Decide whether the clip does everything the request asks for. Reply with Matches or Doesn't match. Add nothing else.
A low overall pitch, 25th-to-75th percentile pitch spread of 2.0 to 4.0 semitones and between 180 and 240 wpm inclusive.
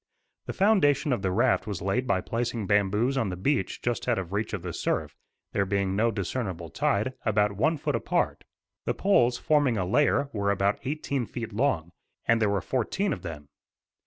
Doesn't match